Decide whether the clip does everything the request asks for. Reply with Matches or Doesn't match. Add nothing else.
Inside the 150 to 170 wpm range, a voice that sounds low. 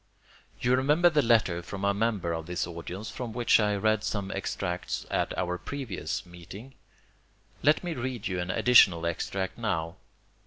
Matches